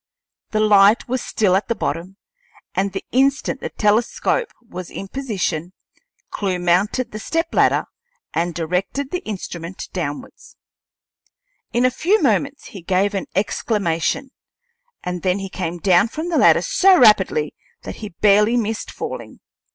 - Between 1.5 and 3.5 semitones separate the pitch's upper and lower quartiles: No, average, 5.2 semitones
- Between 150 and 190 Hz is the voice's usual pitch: No, high, 205 Hz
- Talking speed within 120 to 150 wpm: Yes, average, 145 wpm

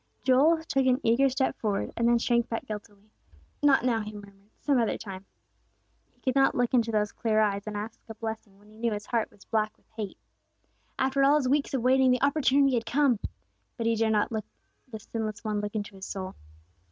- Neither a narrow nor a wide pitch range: Yes, average, 3.6 semitones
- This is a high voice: Yes, high, 225 Hz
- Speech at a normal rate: No, fast, 215 wpm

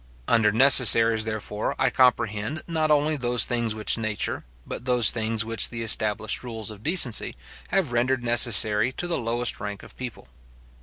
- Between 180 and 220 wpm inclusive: No, average, 160 wpm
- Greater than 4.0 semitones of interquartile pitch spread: No, narrow, 2.6 semitones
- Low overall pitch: Yes, low, 115 Hz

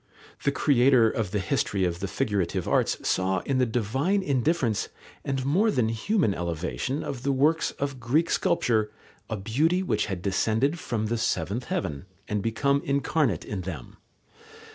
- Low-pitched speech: Yes, low, 120 Hz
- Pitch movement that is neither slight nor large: No, wide, 5.8 semitones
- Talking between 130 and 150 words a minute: No, average, 160 wpm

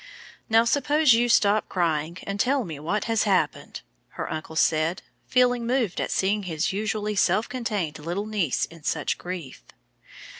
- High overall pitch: Yes, high, 200 Hz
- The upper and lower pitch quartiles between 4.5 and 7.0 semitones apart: Yes, wide, 5.5 semitones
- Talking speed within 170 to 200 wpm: No, average, 155 wpm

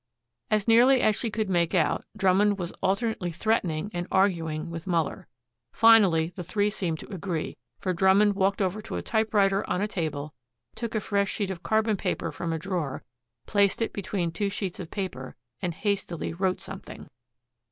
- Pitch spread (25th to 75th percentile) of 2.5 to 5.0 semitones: Yes, average, 3.4 semitones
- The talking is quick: No, average, 175 wpm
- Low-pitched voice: No, high, 190 Hz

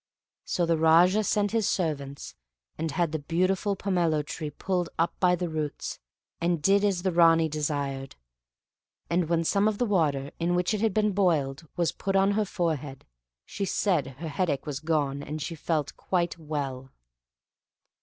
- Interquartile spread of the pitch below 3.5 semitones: No, average, 3.9 semitones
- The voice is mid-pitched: Yes, medium, 165 Hz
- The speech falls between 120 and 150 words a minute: No, average, 170 wpm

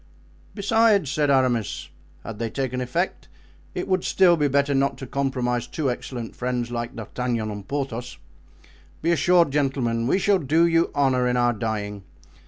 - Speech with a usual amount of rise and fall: Yes, average, 3.7 semitones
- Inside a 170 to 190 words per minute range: No, average, 160 wpm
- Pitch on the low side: Yes, low, 130 Hz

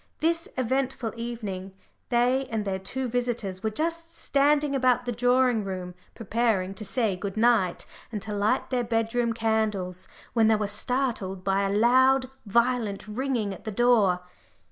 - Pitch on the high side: Yes, high, 230 Hz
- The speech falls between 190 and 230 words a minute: No, average, 160 wpm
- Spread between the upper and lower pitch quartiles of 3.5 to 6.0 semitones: Yes, average, 3.9 semitones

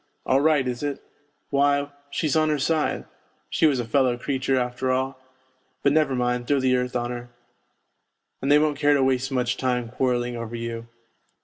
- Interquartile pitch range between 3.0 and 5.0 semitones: No, narrow, 2.6 semitones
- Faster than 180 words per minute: Yes, average, 190 wpm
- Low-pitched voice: Yes, low, 130 Hz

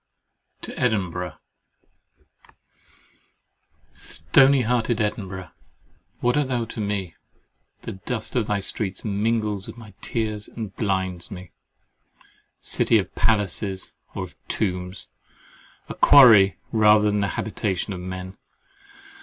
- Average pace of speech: No, slow, 110 wpm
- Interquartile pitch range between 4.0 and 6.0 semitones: No, average, 3.0 semitones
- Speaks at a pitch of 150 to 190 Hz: No, low, 105 Hz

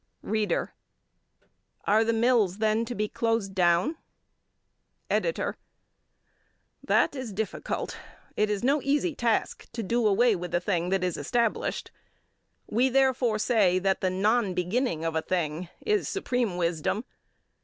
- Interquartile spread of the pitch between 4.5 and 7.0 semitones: Yes, average, 4.8 semitones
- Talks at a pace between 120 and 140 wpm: Yes, slow, 135 wpm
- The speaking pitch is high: Yes, high, 215 Hz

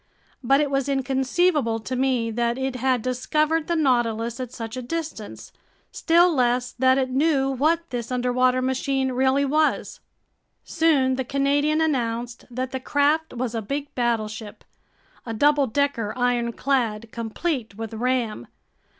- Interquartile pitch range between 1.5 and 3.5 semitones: Yes, average, 3.0 semitones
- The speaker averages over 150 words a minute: No, average, 140 wpm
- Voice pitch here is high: Yes, very high, 255 Hz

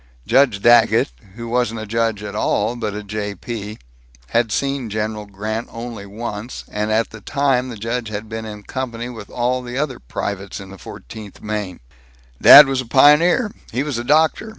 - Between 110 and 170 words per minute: No, average, 185 wpm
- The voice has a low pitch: Yes, low, 115 Hz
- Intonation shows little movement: No, average, 3.0 semitones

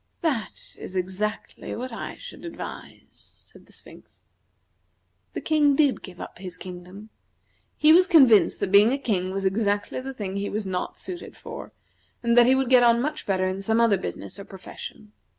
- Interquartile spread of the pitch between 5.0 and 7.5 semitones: Yes, wide, 5.5 semitones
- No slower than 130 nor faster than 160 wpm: No, average, 185 wpm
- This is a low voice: No, high, 215 Hz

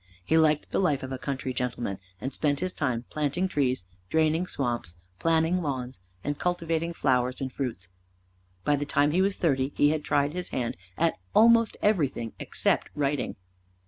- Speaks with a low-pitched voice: No, medium, 145 Hz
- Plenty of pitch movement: No, average, 4.1 semitones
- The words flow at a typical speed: Yes, average, 170 wpm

